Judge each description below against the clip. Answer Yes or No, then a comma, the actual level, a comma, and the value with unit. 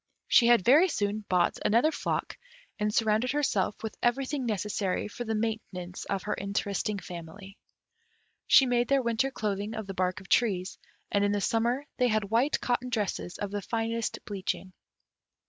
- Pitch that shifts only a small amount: No, average, 3.3 semitones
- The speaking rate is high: No, average, 165 wpm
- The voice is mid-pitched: No, high, 215 Hz